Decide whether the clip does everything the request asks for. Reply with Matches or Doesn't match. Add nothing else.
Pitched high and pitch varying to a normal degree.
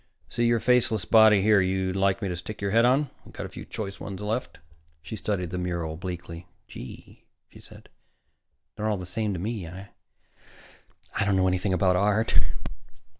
Doesn't match